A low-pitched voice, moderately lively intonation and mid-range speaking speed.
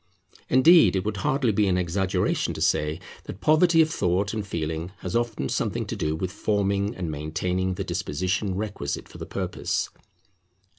Yes: very low, 95 Hz; average, 3.3 semitones; average, 165 wpm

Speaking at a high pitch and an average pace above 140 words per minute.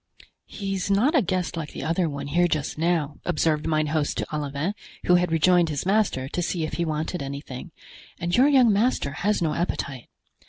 No: medium, 165 Hz; average, 195 wpm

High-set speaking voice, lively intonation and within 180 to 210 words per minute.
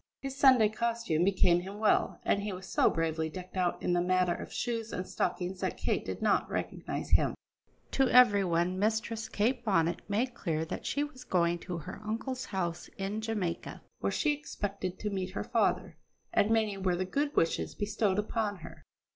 No: high, 200 Hz; average, 4.0 semitones; average, 190 wpm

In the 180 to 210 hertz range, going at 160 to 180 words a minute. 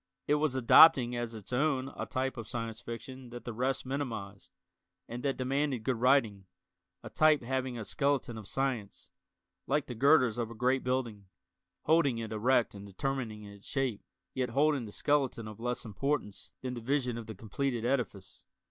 No: low, 125 Hz; average, 175 wpm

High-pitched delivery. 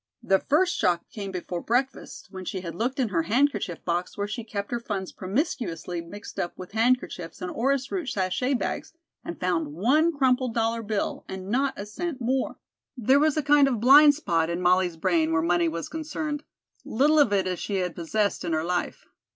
Yes: high, 210 Hz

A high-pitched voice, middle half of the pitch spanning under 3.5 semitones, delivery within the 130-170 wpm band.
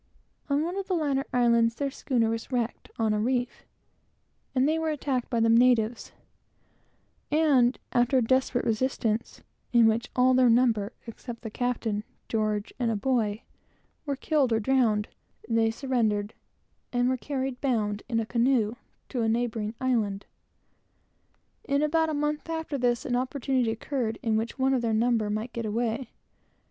Yes: high, 245 Hz; average, 2.9 semitones; average, 160 wpm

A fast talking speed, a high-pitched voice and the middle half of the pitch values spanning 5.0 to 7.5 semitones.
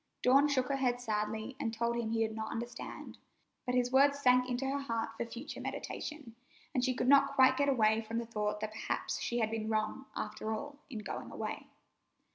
No: fast, 210 wpm; high, 240 Hz; average, 3.3 semitones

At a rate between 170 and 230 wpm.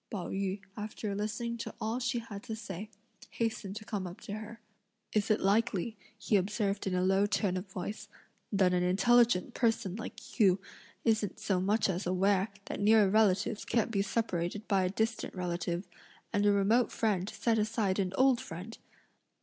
Yes: average, 175 wpm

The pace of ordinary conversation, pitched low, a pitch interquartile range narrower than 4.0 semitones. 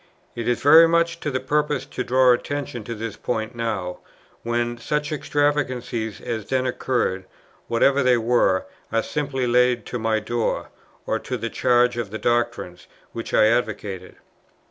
Yes: average, 160 wpm; low, 120 Hz; average, 2.7 semitones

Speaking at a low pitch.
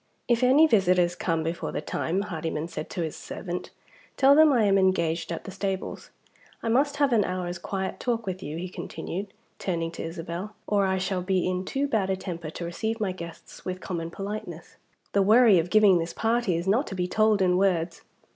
No: high, 190 Hz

